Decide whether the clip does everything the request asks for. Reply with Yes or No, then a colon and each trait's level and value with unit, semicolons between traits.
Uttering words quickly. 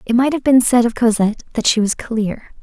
Yes: fast, 250 wpm